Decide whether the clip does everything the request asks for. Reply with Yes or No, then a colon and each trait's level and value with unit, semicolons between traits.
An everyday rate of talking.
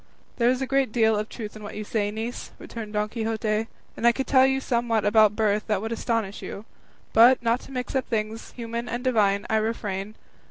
No: fast, 215 wpm